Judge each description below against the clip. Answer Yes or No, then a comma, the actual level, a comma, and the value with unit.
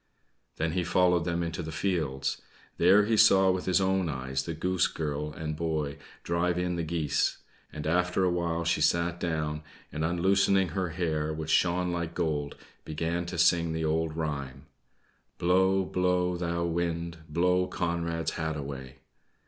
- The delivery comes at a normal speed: Yes, average, 165 wpm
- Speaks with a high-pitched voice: No, very low, 85 Hz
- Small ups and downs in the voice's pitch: Yes, narrow, 2.2 semitones